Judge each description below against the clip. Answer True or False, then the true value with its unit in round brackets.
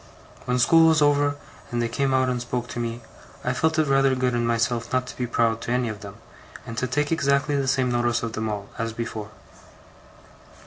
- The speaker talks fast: True (220 wpm)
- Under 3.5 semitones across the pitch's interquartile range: True (2.8 semitones)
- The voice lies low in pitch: True (125 Hz)